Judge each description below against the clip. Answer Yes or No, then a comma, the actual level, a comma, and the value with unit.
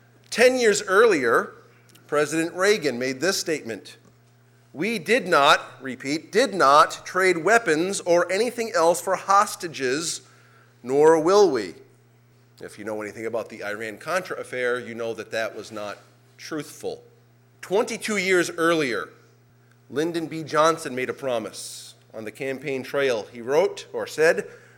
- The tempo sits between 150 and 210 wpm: No, average, 140 wpm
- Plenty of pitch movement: Yes, wide, 7.7 semitones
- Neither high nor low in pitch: Yes, medium, 150 Hz